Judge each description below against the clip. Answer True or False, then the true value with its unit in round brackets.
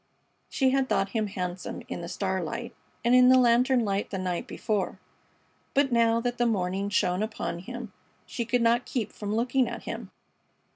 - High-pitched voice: True (230 Hz)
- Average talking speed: True (180 wpm)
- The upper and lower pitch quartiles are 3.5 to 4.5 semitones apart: True (3.9 semitones)